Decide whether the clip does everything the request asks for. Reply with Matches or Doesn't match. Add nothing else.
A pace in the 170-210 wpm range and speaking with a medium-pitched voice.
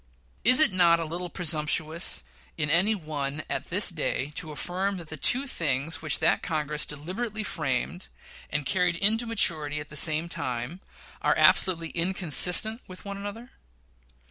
Doesn't match